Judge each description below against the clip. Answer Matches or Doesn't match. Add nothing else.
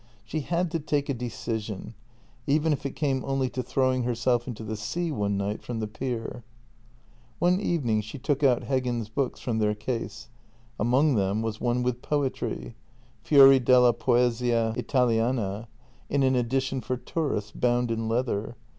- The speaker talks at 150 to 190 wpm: Matches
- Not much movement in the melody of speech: Doesn't match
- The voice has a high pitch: Doesn't match